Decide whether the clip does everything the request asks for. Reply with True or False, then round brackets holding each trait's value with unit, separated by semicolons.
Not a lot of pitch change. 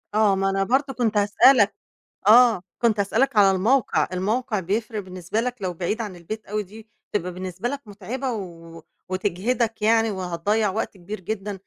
False (3.2 semitones)